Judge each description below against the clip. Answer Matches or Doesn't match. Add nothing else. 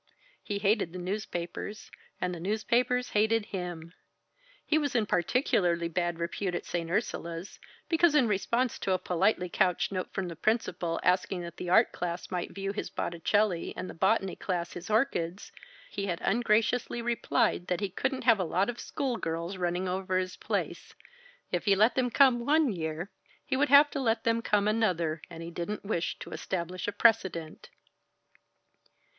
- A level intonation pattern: Doesn't match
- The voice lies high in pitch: Matches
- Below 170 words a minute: Doesn't match